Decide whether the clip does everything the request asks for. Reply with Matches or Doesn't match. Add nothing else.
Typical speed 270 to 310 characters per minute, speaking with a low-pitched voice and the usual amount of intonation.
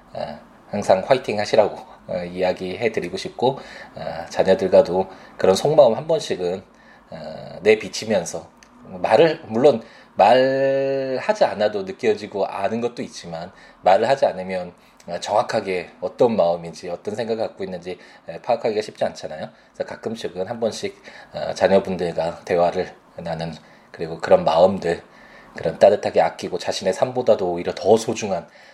Doesn't match